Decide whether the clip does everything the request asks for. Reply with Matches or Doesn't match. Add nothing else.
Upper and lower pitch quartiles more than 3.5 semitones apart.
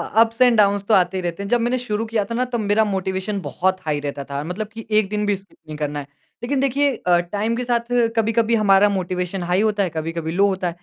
Matches